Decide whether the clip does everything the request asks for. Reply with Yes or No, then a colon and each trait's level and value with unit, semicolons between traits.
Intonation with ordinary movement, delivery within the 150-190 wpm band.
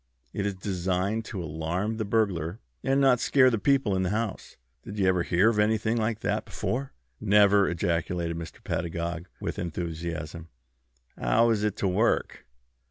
Yes: average, 4.3 semitones; average, 165 wpm